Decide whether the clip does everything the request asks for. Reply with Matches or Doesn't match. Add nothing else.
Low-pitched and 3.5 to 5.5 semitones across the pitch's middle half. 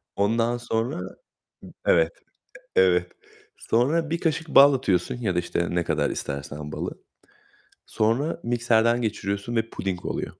Matches